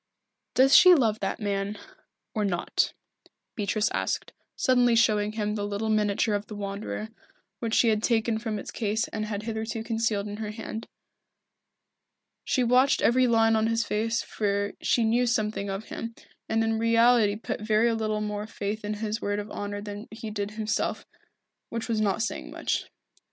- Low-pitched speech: No, high, 220 Hz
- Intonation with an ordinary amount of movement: No, narrow, 1.6 semitones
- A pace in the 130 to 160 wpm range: No, average, 170 wpm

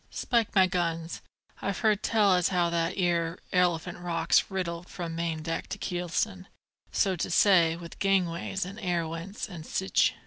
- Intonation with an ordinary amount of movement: No, narrow, 2.3 semitones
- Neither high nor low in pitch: Yes, medium, 175 Hz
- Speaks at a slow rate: No, average, 165 wpm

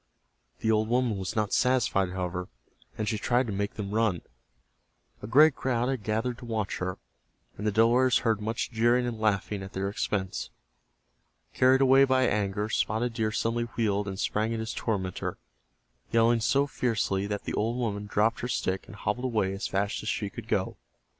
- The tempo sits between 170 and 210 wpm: Yes, average, 185 wpm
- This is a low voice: Yes, low, 110 Hz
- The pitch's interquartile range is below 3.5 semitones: Yes, average, 2.9 semitones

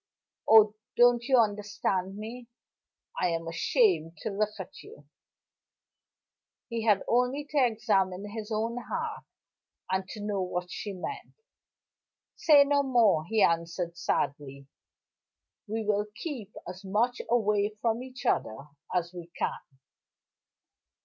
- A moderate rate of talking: No, slow, 125 wpm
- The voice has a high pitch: Yes, high, 210 Hz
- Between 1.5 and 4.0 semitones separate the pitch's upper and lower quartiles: No, average, 4.7 semitones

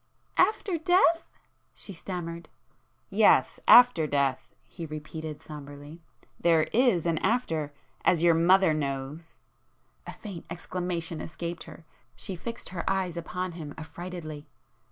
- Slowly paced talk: Yes, slow, 110 wpm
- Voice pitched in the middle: Yes, medium, 170 Hz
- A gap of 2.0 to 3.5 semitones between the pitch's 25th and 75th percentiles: Yes, average, 2.9 semitones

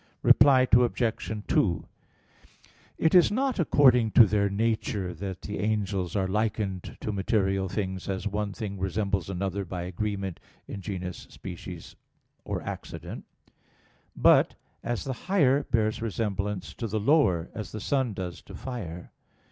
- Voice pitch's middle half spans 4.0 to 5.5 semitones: No, average, 3.3 semitones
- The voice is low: Yes, low, 105 Hz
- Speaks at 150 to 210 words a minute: No, average, 140 wpm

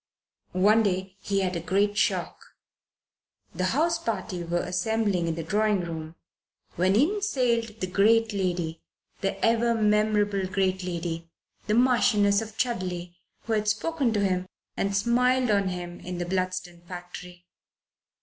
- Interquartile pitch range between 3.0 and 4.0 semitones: Yes, average, 3.7 semitones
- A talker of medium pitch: No, high, 195 Hz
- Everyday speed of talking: Yes, average, 145 wpm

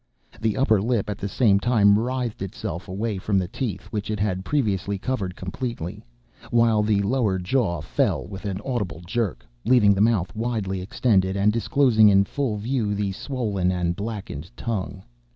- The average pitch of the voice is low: Yes, low, 105 Hz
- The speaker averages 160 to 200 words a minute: Yes, average, 170 wpm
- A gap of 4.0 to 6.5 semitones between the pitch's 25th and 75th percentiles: No, average, 3.5 semitones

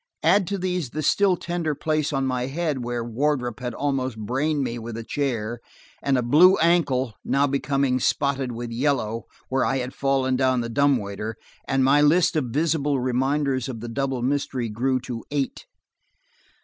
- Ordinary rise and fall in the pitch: Yes, average, 3.2 semitones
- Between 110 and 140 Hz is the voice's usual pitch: Yes, low, 135 Hz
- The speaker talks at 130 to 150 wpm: No, average, 175 wpm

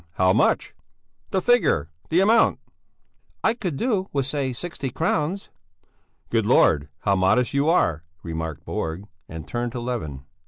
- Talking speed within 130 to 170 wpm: Yes, average, 145 wpm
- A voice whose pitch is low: Yes, low, 125 Hz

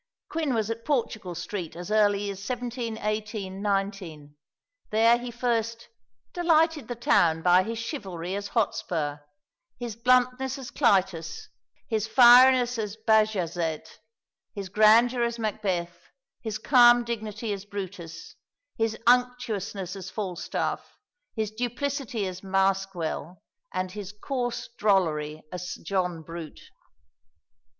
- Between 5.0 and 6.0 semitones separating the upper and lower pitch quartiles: No, average, 4.3 semitones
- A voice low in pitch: No, high, 215 Hz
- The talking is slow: Yes, slow, 115 wpm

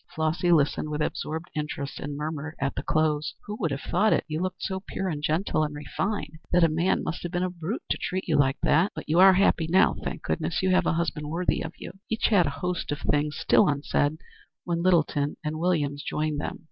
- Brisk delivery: Yes, fast, 230 wpm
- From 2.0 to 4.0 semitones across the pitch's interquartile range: Yes, average, 3.3 semitones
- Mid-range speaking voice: Yes, medium, 160 Hz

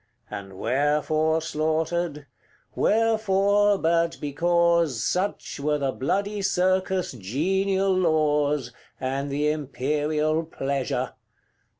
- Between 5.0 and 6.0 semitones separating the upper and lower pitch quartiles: No, average, 4.5 semitones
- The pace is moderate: No, slow, 85 wpm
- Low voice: No, medium, 155 Hz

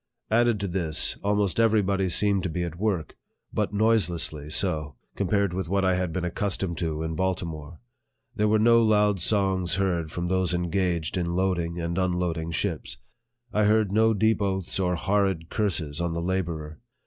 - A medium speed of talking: Yes, average, 170 wpm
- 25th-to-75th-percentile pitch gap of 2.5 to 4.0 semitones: Yes, average, 3.2 semitones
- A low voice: Yes, very low, 95 Hz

